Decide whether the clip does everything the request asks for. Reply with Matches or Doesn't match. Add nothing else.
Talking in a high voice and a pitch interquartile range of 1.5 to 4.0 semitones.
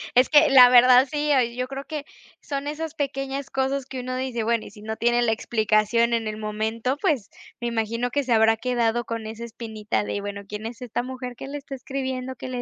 Matches